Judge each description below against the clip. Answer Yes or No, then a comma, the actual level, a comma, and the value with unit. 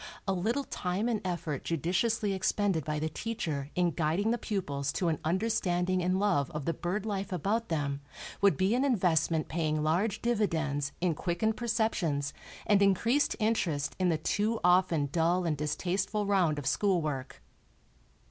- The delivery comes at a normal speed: Yes, average, 160 wpm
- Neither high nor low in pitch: Yes, medium, 180 Hz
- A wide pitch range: No, average, 4.7 semitones